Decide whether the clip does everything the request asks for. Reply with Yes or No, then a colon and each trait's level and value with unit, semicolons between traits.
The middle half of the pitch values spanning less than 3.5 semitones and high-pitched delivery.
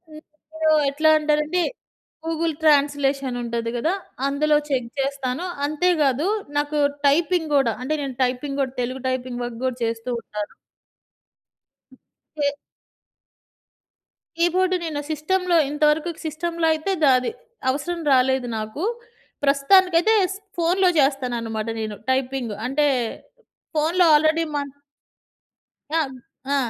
No: average, 3.9 semitones; very high, 290 Hz